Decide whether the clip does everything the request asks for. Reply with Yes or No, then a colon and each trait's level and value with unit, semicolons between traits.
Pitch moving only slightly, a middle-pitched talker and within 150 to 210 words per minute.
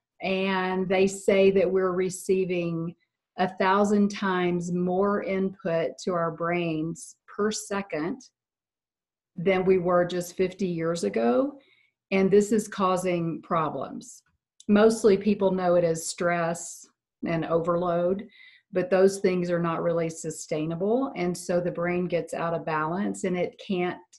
No: narrow, 2.3 semitones; medium, 180 Hz; slow, 135 wpm